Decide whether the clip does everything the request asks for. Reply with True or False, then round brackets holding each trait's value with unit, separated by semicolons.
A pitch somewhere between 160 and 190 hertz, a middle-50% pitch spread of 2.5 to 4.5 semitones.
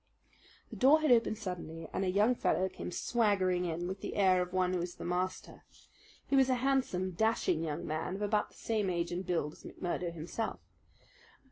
True (185 Hz; 3.8 semitones)